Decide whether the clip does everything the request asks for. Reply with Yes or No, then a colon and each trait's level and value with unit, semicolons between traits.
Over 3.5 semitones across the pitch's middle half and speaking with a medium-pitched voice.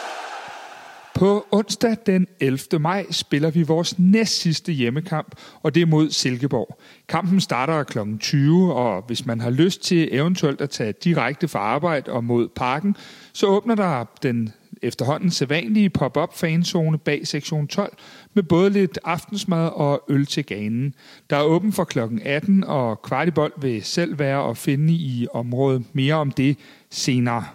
Yes: average, 5.1 semitones; medium, 155 Hz